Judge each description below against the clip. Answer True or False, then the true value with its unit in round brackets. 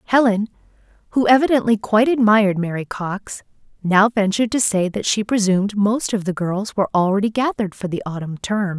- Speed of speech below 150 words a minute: False (170 wpm)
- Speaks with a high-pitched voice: True (205 Hz)